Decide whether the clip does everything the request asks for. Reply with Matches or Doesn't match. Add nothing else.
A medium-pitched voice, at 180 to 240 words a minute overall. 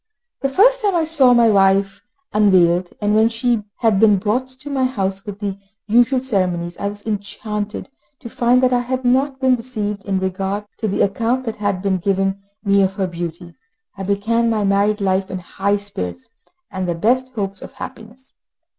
Doesn't match